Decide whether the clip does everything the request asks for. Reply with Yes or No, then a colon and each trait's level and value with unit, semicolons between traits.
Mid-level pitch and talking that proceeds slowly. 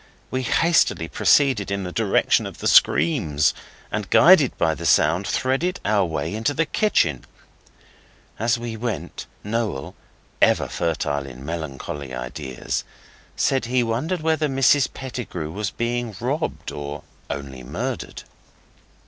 No: low, 105 Hz; slow, 130 wpm